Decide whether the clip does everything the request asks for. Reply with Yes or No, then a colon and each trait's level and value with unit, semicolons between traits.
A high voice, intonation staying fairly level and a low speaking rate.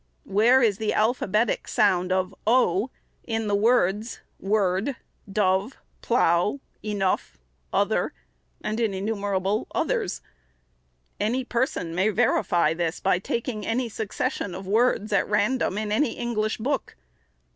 No: high, 210 Hz; average, 3.5 semitones; slow, 125 wpm